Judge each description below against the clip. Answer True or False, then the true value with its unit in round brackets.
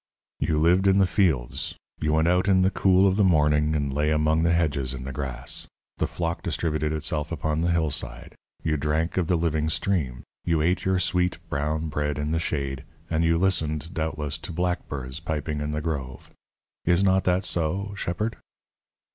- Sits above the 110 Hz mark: False (80 Hz)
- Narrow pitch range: False (3.0 semitones)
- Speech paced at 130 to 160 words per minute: False (185 wpm)